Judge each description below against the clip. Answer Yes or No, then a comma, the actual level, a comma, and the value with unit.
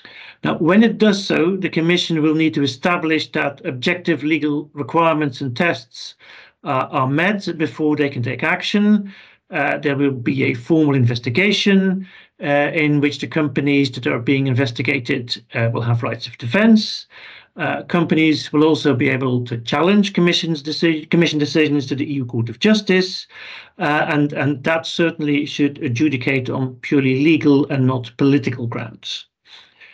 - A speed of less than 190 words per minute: Yes, average, 160 wpm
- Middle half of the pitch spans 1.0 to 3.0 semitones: No, average, 3.5 semitones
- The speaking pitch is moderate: Yes, medium, 150 Hz